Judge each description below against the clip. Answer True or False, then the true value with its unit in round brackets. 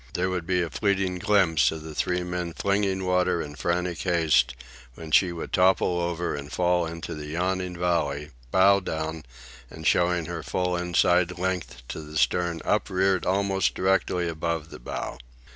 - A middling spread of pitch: False (2.3 semitones)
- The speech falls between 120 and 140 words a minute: False (165 wpm)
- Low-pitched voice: True (90 Hz)